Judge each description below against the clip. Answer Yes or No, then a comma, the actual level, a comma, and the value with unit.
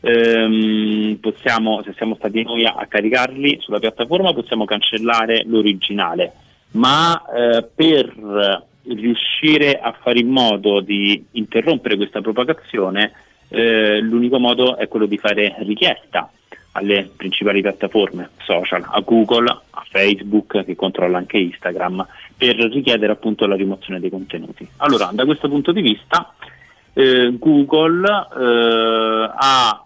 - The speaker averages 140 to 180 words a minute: No, average, 125 wpm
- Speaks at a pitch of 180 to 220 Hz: No, low, 115 Hz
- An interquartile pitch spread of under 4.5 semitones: Yes, average, 3.1 semitones